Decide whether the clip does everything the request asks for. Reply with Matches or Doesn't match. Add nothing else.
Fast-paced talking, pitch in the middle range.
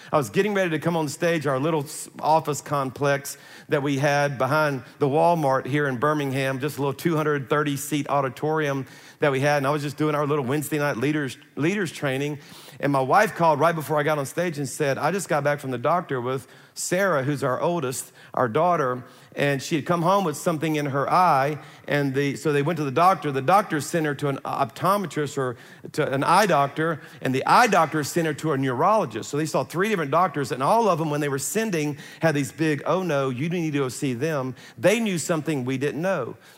Matches